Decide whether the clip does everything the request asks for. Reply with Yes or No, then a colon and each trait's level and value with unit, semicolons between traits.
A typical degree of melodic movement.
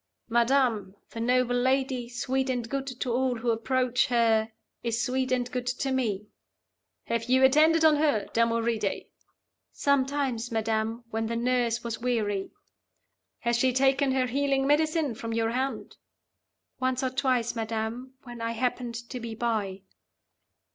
No: narrow, 2.3 semitones